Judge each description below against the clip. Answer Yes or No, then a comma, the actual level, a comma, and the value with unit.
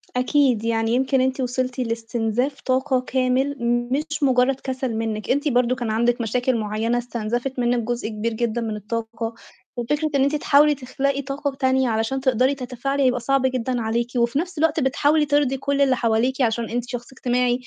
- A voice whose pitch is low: No, very high, 255 Hz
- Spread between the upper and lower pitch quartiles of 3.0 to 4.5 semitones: No, narrow, 2.6 semitones